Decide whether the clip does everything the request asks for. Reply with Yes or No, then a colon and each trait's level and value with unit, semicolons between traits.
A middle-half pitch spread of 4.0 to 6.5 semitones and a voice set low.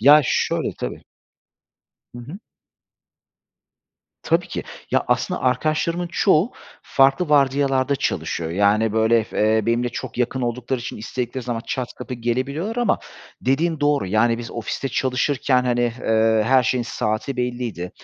No: average, 3.2 semitones; low, 125 Hz